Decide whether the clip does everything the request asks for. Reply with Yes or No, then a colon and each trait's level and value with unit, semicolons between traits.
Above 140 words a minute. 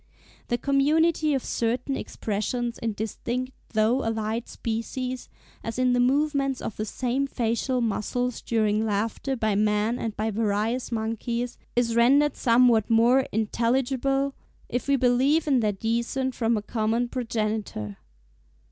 No: slow, 135 wpm